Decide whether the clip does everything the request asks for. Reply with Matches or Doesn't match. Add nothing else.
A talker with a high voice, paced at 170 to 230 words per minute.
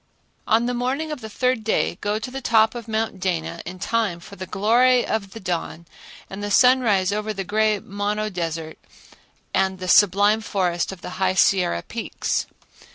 Matches